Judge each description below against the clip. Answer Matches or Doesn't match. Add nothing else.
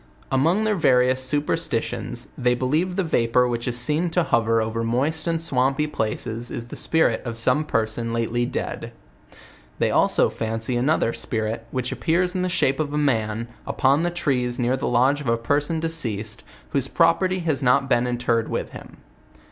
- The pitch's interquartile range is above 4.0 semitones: Matches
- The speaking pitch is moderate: Doesn't match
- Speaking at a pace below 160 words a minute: Doesn't match